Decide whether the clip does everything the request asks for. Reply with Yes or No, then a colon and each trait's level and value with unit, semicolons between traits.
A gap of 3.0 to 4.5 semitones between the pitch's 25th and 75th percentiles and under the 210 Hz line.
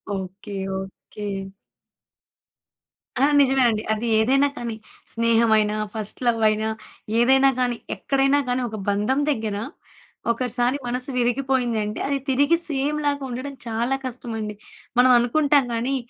No: average, 3.5 semitones; high, 245 Hz